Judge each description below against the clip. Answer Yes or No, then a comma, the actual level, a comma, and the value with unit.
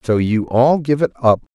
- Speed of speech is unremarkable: No, fast, 235 wpm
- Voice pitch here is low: Yes, low, 125 Hz